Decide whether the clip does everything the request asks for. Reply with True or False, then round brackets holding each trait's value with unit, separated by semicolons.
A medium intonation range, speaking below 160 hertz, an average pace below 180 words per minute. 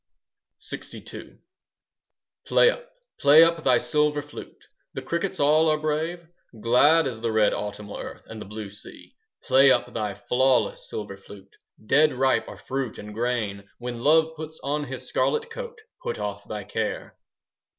False (6.2 semitones; 135 Hz; 160 wpm)